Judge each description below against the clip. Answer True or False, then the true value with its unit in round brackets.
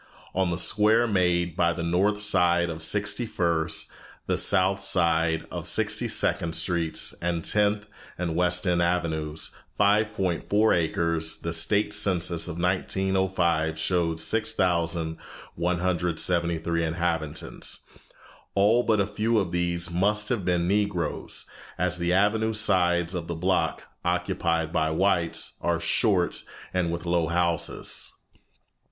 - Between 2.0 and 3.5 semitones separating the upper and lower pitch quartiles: True (2.6 semitones)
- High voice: False (90 Hz)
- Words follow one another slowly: True (125 wpm)